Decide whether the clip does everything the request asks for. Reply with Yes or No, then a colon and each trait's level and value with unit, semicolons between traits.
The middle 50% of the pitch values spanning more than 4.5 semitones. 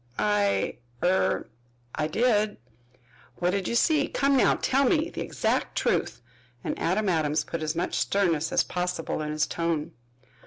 Yes: average, 5.0 semitones